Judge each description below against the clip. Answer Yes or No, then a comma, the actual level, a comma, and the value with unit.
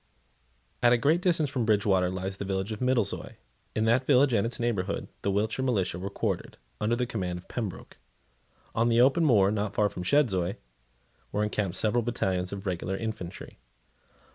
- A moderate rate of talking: Yes, average, 175 wpm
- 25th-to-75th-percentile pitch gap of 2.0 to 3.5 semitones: No, average, 4.0 semitones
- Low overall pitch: Yes, low, 105 Hz